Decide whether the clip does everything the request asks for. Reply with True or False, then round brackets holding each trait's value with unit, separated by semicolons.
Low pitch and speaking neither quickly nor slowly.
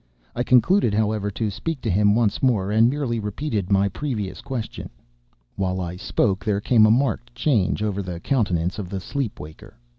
True (105 Hz; 180 wpm)